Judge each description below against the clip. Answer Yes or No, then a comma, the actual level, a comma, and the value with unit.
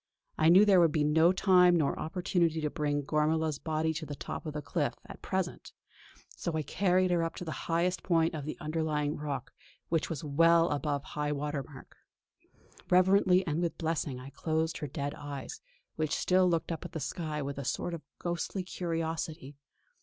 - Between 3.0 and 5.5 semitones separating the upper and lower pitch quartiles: No, narrow, 2.5 semitones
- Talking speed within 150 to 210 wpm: Yes, average, 190 wpm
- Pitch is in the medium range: Yes, medium, 160 Hz